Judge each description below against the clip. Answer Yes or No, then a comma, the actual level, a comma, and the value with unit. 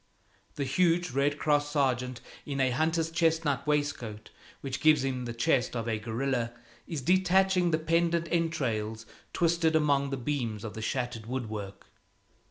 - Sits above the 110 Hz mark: Yes, medium, 140 Hz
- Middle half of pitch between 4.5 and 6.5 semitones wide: Yes, average, 5.1 semitones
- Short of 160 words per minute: Yes, average, 150 wpm